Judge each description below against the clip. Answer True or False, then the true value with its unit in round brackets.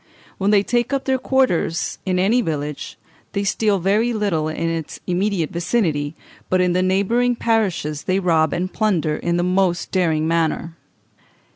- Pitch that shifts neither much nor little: True (4.2 semitones)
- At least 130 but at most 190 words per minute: True (160 wpm)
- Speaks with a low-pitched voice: False (185 Hz)